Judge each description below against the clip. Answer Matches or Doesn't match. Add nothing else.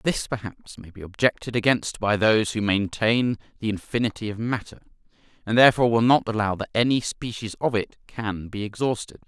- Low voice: Matches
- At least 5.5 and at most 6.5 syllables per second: Matches